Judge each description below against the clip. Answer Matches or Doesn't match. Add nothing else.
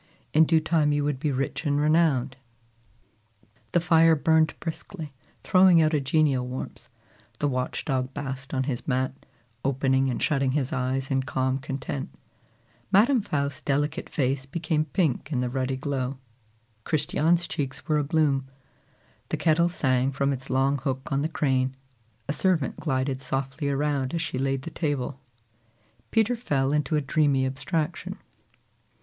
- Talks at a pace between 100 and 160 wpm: Matches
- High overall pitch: Doesn't match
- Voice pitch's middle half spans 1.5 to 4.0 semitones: Matches